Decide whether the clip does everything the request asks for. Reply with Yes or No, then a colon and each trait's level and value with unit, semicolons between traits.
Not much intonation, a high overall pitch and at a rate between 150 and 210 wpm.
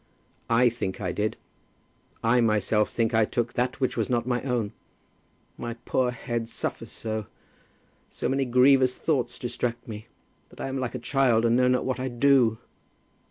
No: narrow, 2.1 semitones; low, 120 Hz; average, 170 wpm